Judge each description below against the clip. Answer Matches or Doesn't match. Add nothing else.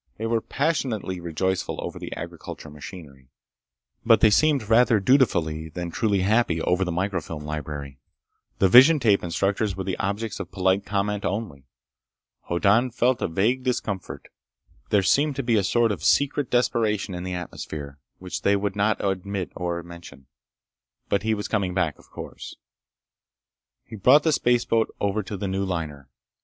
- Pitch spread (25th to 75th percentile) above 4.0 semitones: Matches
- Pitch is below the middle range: Matches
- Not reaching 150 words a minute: Doesn't match